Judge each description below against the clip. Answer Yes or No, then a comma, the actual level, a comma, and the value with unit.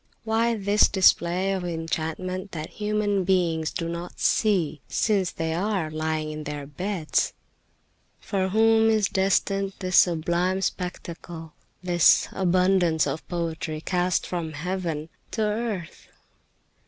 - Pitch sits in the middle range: Yes, medium, 180 Hz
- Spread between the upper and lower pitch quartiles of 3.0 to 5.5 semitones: Yes, average, 3.3 semitones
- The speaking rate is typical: No, slow, 120 wpm